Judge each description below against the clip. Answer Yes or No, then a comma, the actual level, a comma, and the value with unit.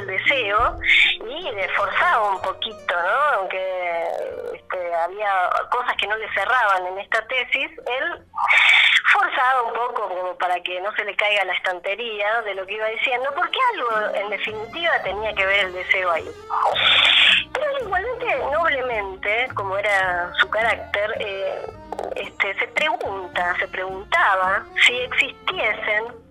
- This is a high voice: Yes, high, 215 Hz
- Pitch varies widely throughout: Yes, wide, 7.6 semitones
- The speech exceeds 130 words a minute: Yes, average, 145 wpm